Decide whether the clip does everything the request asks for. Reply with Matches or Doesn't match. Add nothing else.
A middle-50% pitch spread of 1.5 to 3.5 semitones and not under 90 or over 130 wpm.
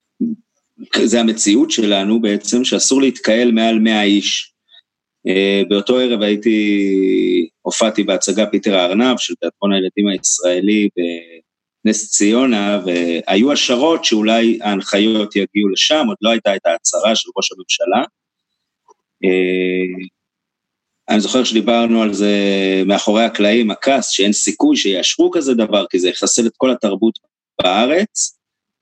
Matches